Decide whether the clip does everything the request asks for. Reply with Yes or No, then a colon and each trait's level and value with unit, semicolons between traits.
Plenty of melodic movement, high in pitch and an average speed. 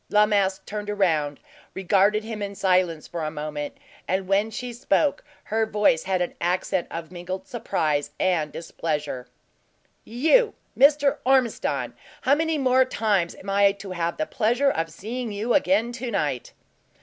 Yes: wide, 5.7 semitones; high, 200 Hz; average, 155 wpm